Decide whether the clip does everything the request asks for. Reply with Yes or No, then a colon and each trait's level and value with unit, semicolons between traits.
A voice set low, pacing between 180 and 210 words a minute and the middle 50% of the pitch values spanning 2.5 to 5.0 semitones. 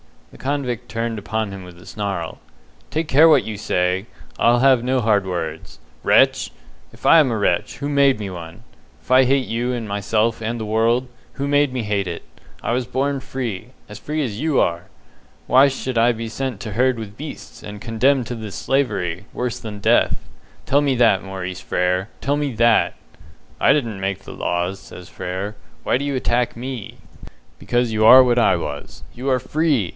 Yes: low, 115 Hz; average, 195 wpm; average, 4.5 semitones